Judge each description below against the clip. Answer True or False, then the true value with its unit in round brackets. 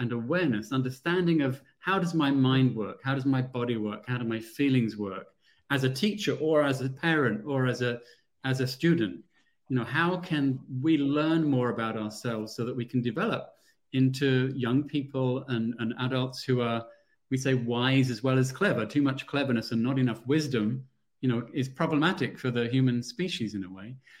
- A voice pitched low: True (130 Hz)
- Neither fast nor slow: True (195 wpm)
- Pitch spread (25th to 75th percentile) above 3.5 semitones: False (2.9 semitones)